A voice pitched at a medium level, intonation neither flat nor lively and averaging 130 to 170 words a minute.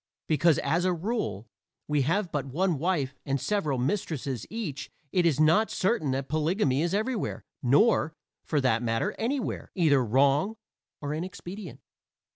No: medium, 155 Hz; wide, 5.7 semitones; average, 145 wpm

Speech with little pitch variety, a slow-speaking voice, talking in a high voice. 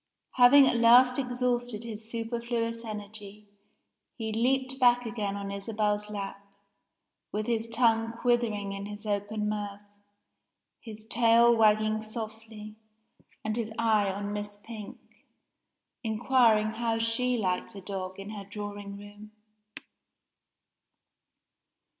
Yes: narrow, 2.1 semitones; slow, 115 wpm; high, 220 Hz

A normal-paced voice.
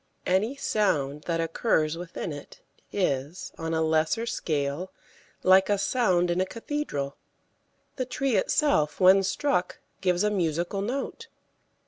No: slow, 130 wpm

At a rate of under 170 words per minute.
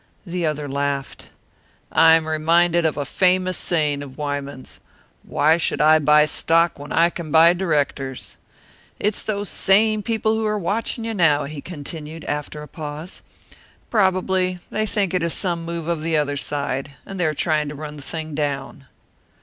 No: average, 175 wpm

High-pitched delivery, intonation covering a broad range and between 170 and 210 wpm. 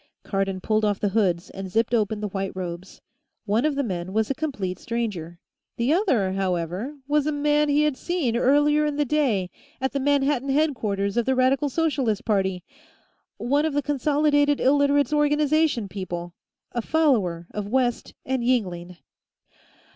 No: high, 245 Hz; wide, 6.9 semitones; average, 160 wpm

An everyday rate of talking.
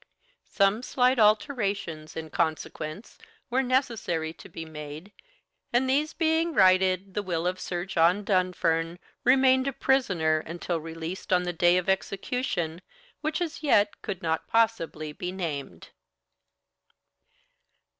No: slow, 125 wpm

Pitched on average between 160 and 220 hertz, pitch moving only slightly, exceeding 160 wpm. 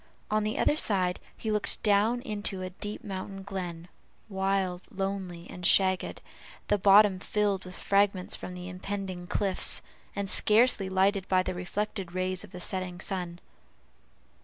No: high, 190 Hz; narrow, 1.9 semitones; average, 150 wpm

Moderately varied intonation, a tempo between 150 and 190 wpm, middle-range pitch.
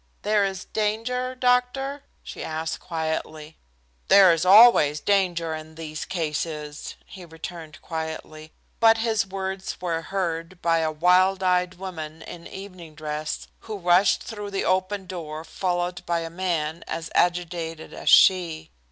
No: average, 3.2 semitones; average, 140 wpm; medium, 175 Hz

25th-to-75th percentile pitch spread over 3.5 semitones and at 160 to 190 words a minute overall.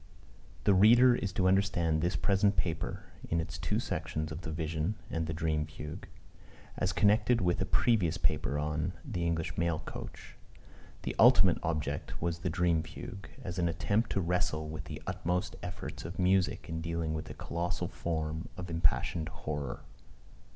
No: average, 3.1 semitones; average, 170 wpm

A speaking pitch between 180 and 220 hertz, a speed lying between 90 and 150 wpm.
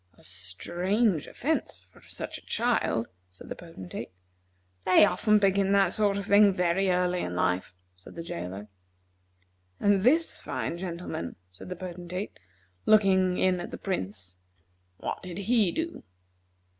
Yes: medium, 185 Hz; average, 145 wpm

